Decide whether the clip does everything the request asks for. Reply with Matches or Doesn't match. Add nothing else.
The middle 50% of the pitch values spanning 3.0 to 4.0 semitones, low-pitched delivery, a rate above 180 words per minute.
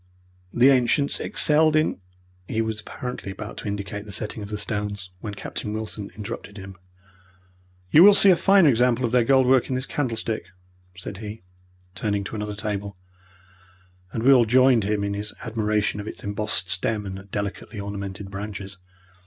Doesn't match